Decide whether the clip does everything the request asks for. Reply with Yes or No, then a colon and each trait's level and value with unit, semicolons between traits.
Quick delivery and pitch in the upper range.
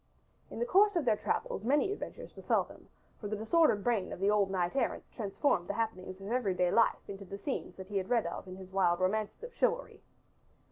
Yes: fast, 225 wpm; high, 210 Hz